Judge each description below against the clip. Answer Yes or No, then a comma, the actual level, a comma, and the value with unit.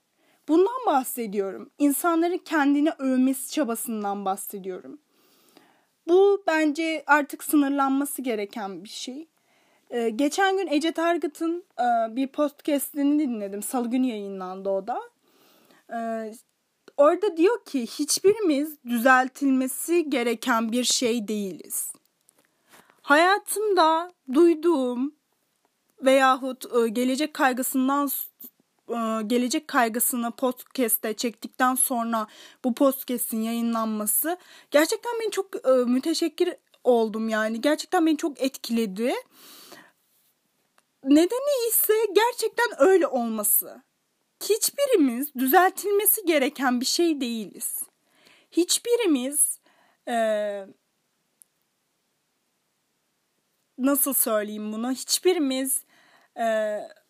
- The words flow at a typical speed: No, slow, 80 wpm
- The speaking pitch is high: Yes, very high, 275 Hz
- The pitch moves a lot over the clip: Yes, wide, 5.7 semitones